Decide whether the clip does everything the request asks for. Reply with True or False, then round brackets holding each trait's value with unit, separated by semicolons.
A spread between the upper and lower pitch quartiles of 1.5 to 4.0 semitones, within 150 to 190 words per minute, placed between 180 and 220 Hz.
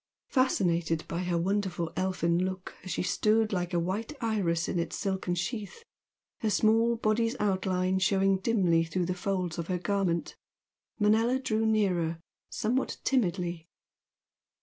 False (3.5 semitones; 140 wpm; 190 Hz)